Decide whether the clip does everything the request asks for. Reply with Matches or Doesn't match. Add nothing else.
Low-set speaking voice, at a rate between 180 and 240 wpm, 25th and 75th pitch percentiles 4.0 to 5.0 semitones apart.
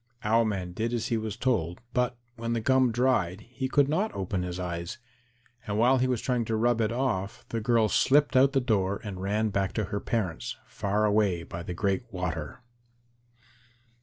Matches